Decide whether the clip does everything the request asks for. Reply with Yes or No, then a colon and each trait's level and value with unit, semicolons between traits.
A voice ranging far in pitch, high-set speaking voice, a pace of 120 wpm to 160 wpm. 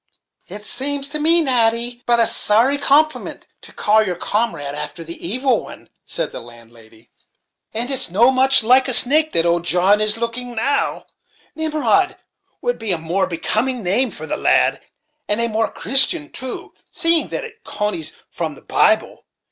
No: wide, 6.1 semitones; high, 235 Hz; average, 170 wpm